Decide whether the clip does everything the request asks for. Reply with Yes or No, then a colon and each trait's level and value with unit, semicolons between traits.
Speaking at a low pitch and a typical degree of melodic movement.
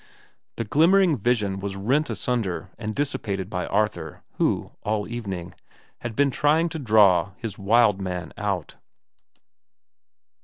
Yes: low, 105 Hz; average, 4.3 semitones